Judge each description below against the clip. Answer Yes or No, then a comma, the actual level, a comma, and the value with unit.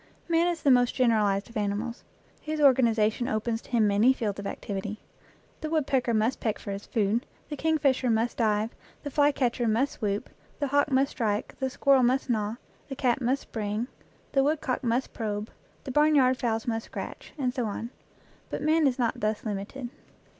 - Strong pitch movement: No, average, 3.9 semitones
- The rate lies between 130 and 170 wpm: No, average, 180 wpm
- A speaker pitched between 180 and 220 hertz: No, high, 240 Hz